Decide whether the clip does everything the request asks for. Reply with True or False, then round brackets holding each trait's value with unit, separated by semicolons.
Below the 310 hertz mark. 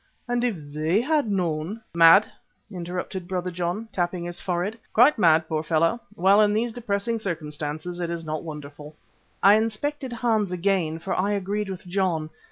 True (185 Hz)